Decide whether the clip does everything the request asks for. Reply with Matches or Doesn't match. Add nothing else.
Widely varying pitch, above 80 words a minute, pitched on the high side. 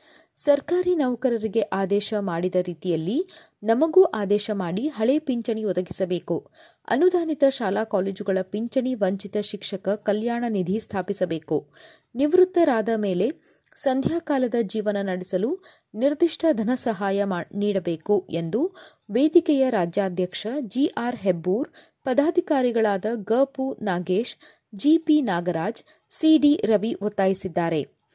Matches